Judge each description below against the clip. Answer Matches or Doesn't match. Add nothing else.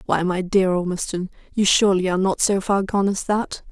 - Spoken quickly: Matches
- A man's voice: Doesn't match